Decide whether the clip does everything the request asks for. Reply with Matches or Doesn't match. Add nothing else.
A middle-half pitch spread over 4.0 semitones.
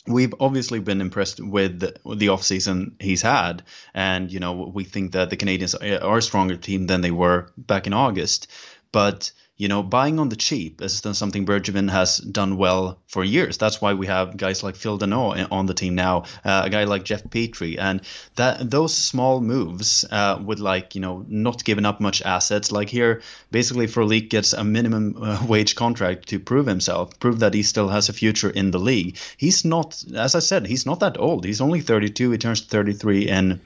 Doesn't match